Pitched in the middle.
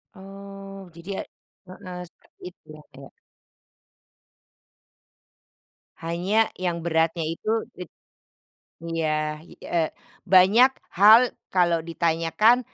Yes: medium, 175 Hz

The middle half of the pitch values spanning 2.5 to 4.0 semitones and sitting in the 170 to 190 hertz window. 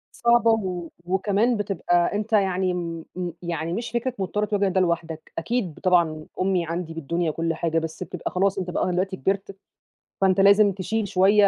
Yes: average, 3.0 semitones; medium, 185 Hz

